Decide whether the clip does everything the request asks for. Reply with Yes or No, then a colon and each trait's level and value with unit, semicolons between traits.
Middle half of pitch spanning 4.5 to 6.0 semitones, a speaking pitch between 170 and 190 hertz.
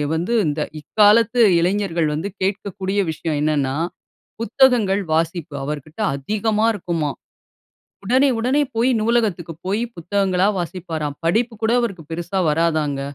Yes: average, 5.0 semitones; medium, 185 Hz